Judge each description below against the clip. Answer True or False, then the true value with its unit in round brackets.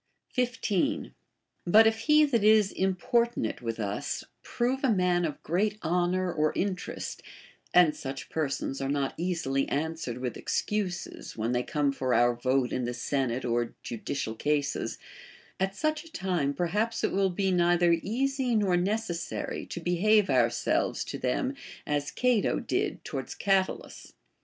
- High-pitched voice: False (175 Hz)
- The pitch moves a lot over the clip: True (7.5 semitones)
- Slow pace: False (145 wpm)